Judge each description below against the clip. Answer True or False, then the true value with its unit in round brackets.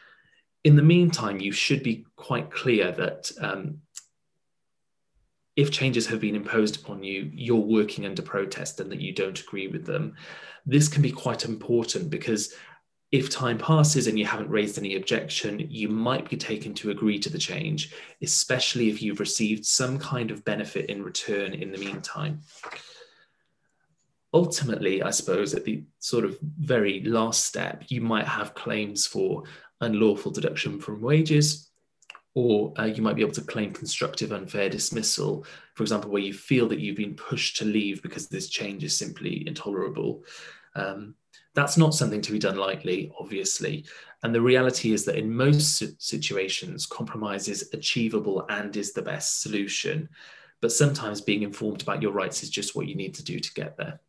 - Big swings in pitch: True (6.0 semitones)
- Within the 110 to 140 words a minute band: False (170 wpm)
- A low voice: True (115 Hz)